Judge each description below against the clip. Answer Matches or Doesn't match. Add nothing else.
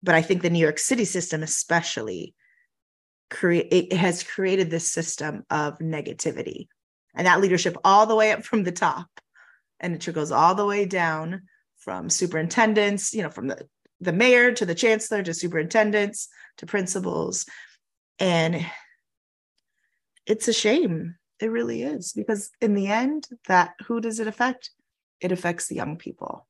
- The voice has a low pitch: Doesn't match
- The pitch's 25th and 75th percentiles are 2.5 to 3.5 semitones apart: Doesn't match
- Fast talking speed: Doesn't match